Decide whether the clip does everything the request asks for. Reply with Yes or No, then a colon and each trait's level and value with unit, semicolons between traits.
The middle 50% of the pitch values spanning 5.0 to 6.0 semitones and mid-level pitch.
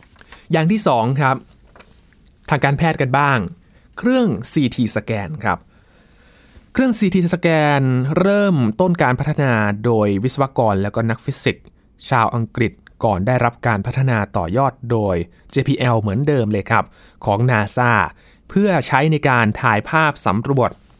No: wide, 5.5 semitones; low, 125 Hz